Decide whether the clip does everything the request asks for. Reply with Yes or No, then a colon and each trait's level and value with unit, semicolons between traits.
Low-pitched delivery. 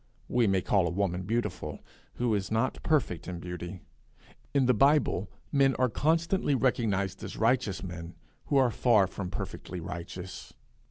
Yes: low, 100 Hz